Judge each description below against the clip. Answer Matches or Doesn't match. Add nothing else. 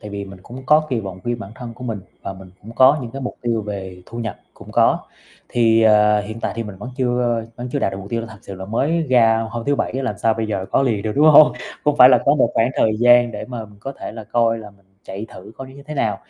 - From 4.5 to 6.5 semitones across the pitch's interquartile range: Doesn't match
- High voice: Doesn't match